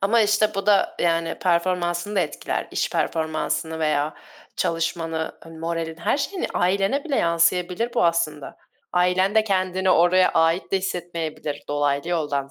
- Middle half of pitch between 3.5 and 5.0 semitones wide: No, average, 2.7 semitones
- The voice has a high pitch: No, medium, 175 Hz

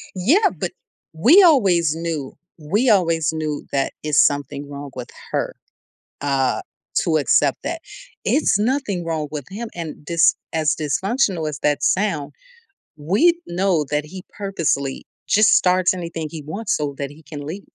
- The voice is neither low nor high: Yes, medium, 165 Hz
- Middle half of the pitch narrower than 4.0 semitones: No, average, 5.1 semitones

